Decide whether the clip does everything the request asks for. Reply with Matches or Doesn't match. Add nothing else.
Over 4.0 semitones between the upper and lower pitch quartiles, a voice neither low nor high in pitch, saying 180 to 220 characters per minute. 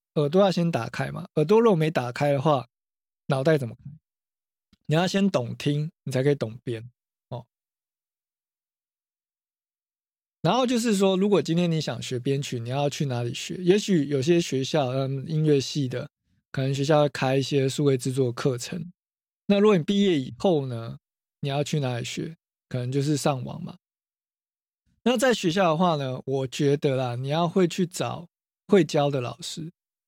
Doesn't match